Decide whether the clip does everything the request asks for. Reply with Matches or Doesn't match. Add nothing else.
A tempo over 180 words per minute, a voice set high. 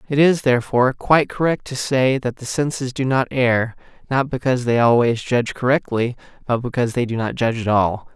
Doesn't match